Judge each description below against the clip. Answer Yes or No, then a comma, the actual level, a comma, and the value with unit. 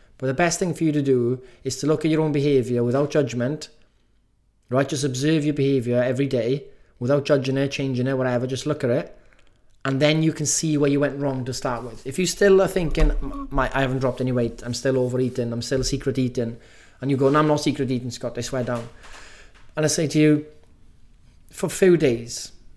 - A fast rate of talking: Yes, fast, 220 wpm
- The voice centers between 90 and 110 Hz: No, low, 135 Hz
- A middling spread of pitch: Yes, average, 3.4 semitones